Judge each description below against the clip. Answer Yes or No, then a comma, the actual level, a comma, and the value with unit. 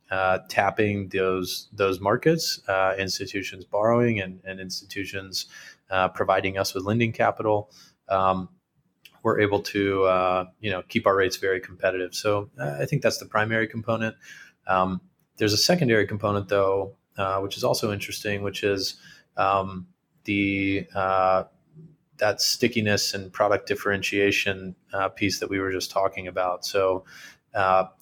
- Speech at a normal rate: Yes, average, 145 wpm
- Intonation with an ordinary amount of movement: No, narrow, 1.9 semitones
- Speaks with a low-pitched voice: Yes, low, 100 Hz